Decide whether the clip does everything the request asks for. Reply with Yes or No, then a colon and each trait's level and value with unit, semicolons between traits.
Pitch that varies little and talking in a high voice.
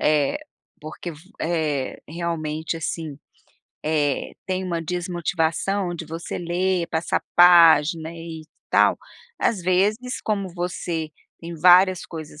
No: narrow, 2.2 semitones; medium, 170 Hz